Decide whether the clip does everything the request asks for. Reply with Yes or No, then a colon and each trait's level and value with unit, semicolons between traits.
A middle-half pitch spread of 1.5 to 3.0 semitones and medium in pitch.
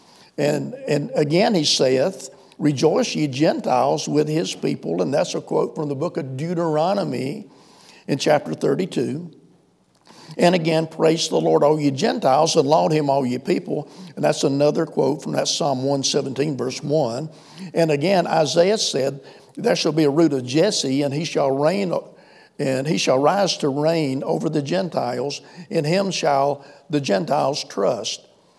Yes: average, 2.7 semitones; medium, 155 Hz